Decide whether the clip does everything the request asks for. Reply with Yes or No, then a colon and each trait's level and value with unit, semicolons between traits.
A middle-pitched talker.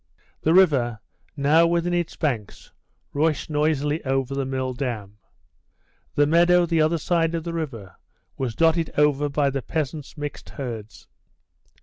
Yes: medium, 150 Hz